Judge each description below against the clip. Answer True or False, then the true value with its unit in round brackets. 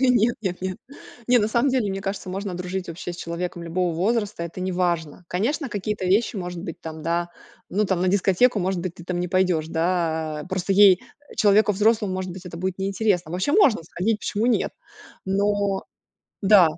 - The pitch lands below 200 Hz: True (185 Hz)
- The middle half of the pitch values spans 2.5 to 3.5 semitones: True (2.8 semitones)